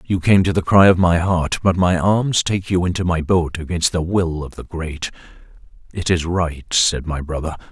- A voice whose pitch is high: No, very low, 85 Hz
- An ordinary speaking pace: No, fast, 220 wpm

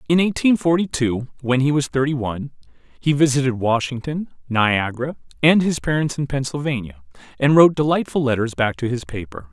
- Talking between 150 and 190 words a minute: Yes, average, 165 wpm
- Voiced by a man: Yes, male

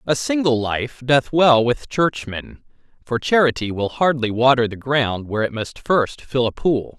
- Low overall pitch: Yes, low, 130 Hz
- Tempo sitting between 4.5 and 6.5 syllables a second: No, 4.3 syllables/s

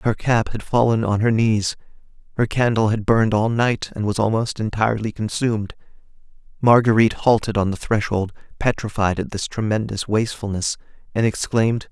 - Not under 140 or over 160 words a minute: Yes, average, 150 wpm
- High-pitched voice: No, low, 110 Hz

